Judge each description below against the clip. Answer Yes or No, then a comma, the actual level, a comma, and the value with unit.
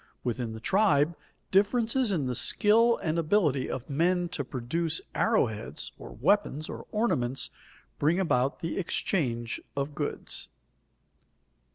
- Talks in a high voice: No, medium, 160 Hz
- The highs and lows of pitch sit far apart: Yes, wide, 6.9 semitones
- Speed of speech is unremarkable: No, slow, 130 wpm